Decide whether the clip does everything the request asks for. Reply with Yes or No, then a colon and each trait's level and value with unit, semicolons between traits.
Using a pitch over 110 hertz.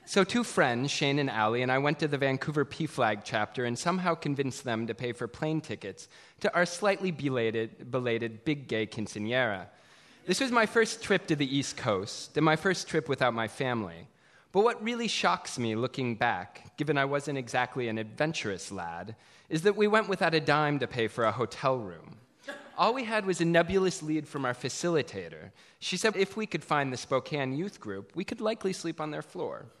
Yes: medium, 140 Hz